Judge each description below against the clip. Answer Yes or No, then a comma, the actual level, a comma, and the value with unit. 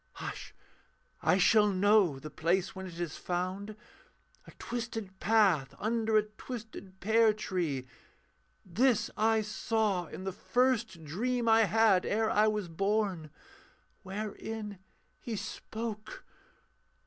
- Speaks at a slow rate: Yes, slow, 120 wpm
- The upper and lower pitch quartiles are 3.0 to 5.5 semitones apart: Yes, average, 3.3 semitones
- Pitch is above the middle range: Yes, high, 210 Hz